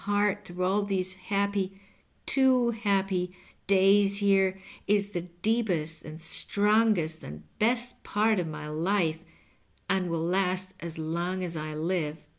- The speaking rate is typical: Yes, average, 150 wpm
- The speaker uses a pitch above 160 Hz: Yes, high, 190 Hz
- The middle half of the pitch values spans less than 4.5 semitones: Yes, average, 3.3 semitones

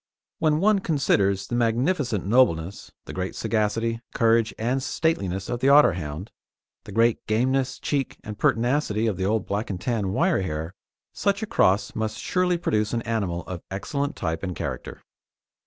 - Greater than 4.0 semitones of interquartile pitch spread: Yes, average, 5.3 semitones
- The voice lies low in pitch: Yes, low, 110 Hz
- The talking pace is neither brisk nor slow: Yes, average, 160 wpm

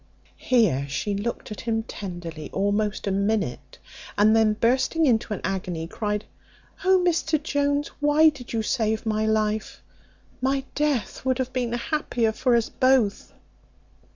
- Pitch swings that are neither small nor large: Yes, average, 4.1 semitones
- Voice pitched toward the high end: Yes, high, 225 Hz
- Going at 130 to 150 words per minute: Yes, average, 145 wpm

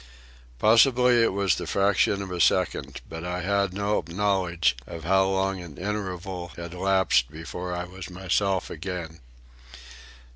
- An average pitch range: No, narrow, 2.3 semitones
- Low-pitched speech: Yes, very low, 95 Hz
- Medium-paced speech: Yes, average, 145 wpm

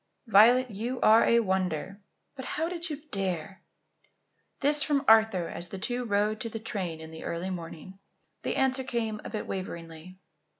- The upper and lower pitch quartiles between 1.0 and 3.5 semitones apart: No, average, 5.0 semitones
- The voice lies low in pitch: No, high, 210 Hz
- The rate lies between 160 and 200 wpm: Yes, average, 170 wpm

